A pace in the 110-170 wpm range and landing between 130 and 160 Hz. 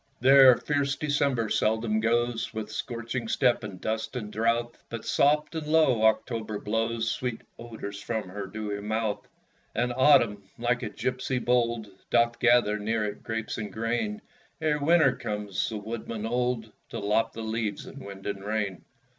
No: average, 160 wpm; low, 115 Hz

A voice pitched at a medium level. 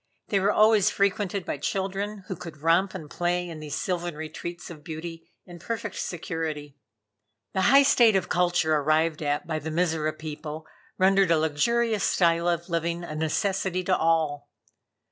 Yes: medium, 170 Hz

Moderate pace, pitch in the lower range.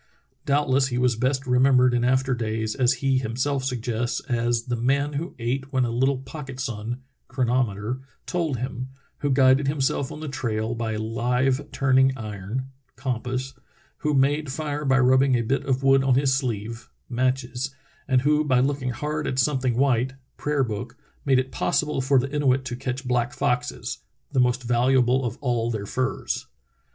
Yes: average, 175 wpm; low, 130 Hz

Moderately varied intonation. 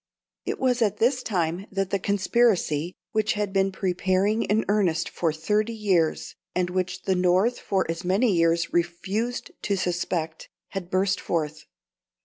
Yes: average, 3.2 semitones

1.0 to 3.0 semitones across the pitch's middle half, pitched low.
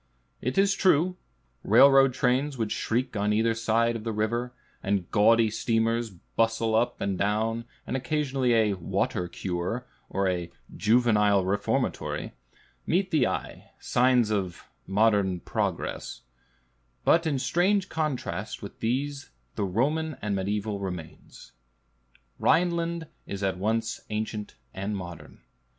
No: average, 4.5 semitones; low, 115 Hz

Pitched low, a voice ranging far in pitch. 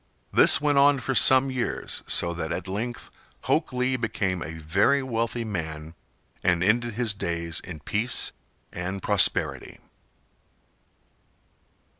Yes: low, 105 Hz; wide, 6.4 semitones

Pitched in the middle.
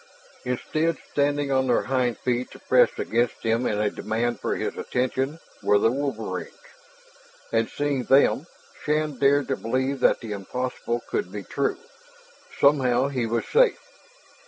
No: low, 125 Hz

